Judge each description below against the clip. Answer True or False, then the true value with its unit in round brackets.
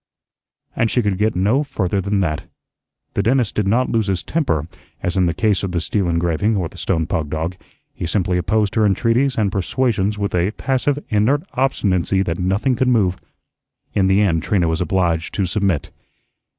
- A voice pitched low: True (100 Hz)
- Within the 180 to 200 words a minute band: True (190 wpm)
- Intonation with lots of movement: False (3.8 semitones)